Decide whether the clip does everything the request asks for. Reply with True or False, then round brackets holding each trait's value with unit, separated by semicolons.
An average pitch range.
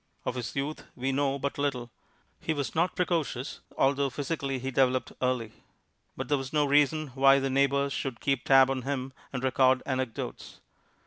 False (1.5 semitones)